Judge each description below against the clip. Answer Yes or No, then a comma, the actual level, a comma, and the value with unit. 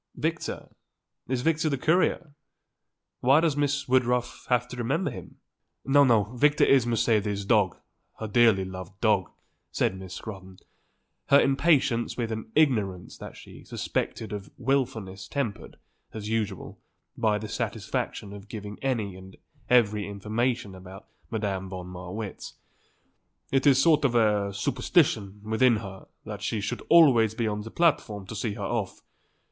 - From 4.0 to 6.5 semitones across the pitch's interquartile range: Yes, average, 4.4 semitones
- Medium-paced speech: Yes, average, 145 wpm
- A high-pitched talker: No, low, 110 Hz